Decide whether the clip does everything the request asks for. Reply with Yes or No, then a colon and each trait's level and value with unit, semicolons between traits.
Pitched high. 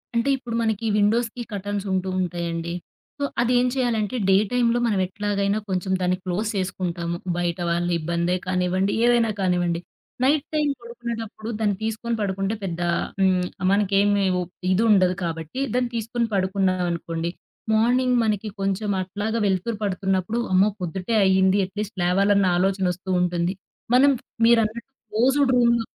Yes: high, 200 Hz